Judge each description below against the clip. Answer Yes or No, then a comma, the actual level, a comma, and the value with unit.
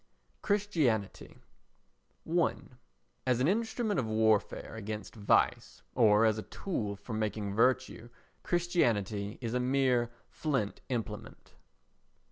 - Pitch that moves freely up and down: No, average, 4.4 semitones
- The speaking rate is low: Yes, slow, 105 wpm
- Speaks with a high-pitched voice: No, low, 115 Hz